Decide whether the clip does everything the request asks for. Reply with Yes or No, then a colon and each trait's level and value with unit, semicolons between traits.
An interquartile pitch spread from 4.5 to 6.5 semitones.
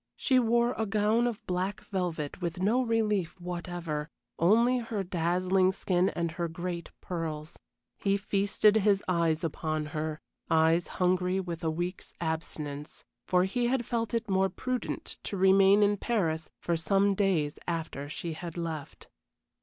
No: average, 3.7 semitones